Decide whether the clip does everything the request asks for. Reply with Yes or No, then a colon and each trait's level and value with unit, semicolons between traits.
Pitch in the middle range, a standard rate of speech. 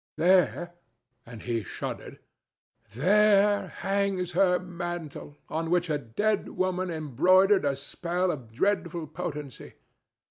No: medium, 175 Hz; slow, 100 wpm